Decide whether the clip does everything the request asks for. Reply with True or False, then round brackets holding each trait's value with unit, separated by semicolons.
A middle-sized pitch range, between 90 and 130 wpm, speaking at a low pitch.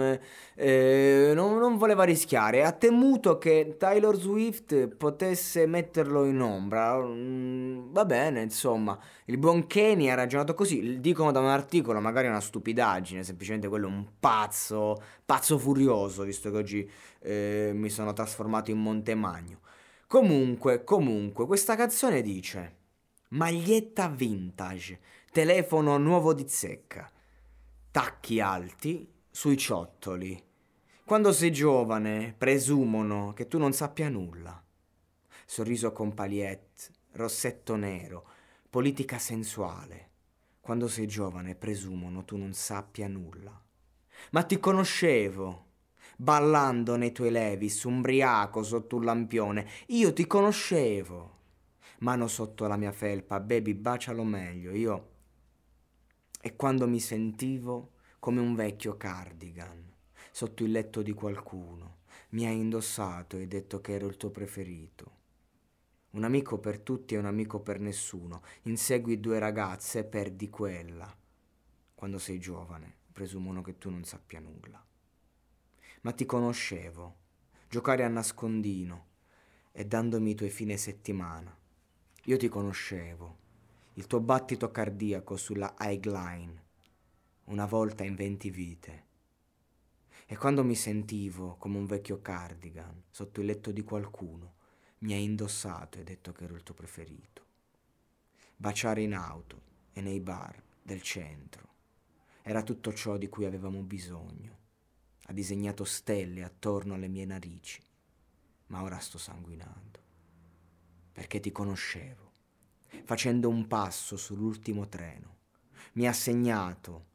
True (4.5 semitones; 125 wpm; 105 Hz)